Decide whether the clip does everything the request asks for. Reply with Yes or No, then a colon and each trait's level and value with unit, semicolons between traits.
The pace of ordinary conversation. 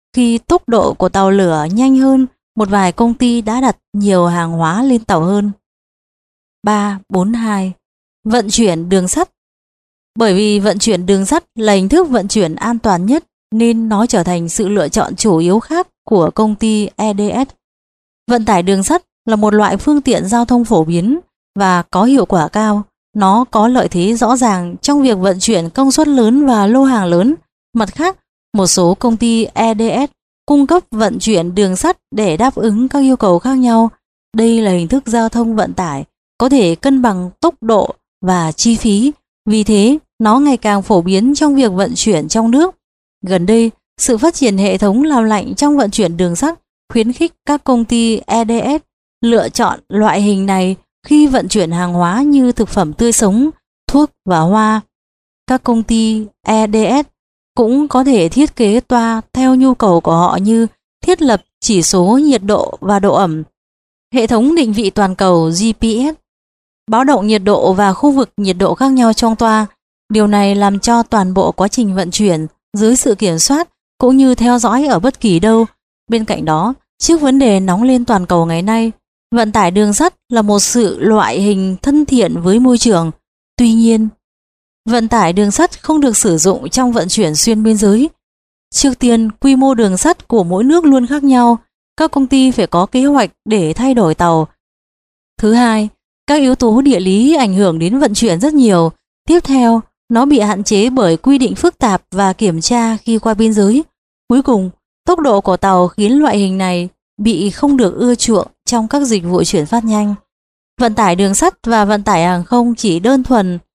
Yes: average, 200 wpm